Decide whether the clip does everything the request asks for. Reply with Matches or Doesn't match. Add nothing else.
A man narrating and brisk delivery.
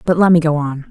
Doesn't match